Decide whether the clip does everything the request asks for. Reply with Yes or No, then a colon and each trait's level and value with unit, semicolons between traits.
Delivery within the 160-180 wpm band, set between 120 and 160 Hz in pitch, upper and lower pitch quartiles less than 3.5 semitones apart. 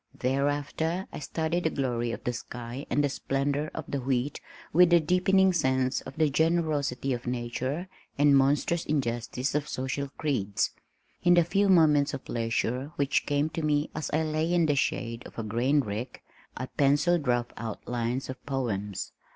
No: average, 170 wpm; medium, 140 Hz; average, 4.0 semitones